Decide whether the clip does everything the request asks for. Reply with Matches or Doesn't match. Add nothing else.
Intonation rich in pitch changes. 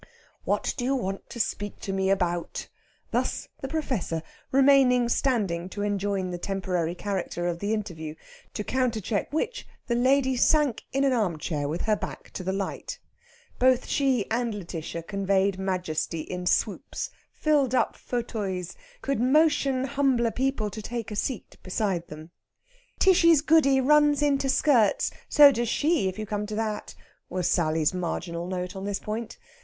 Matches